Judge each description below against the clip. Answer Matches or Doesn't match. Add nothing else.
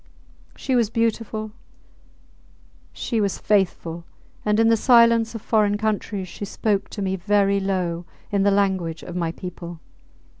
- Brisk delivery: Doesn't match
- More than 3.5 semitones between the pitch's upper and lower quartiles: Doesn't match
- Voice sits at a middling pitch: Doesn't match